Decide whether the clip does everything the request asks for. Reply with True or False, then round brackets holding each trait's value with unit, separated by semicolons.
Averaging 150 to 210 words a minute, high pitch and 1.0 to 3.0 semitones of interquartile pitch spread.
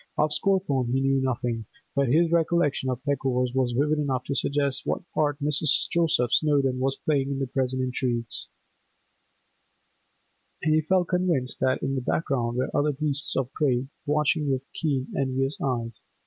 False (165 wpm; 135 Hz; 2.7 semitones)